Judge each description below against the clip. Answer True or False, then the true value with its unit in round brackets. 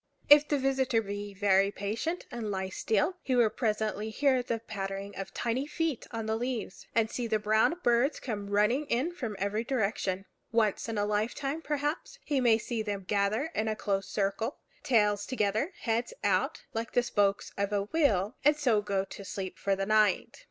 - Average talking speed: True (185 wpm)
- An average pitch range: True (4.0 semitones)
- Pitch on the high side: True (220 Hz)